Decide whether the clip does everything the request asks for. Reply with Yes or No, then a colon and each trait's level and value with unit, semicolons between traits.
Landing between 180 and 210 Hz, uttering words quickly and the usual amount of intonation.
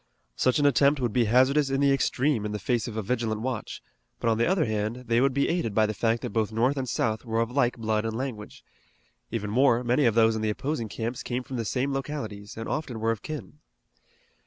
No: low, 120 Hz; fast, 240 wpm; average, 3.4 semitones